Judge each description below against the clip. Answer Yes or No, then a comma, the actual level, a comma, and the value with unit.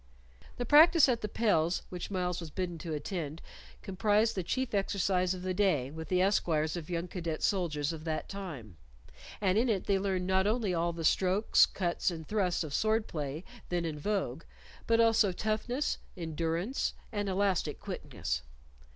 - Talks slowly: No, average, 170 wpm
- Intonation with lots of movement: No, average, 4.0 semitones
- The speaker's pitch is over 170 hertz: Yes, medium, 185 Hz